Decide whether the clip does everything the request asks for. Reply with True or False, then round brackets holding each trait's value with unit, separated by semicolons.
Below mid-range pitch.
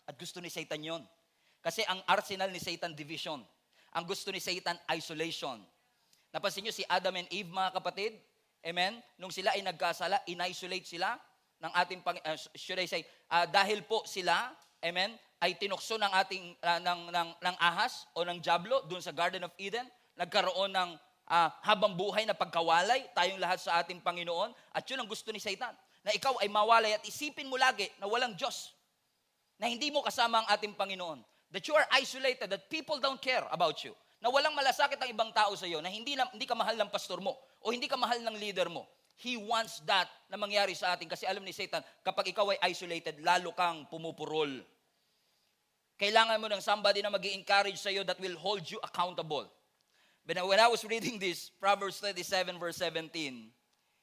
False (190 Hz)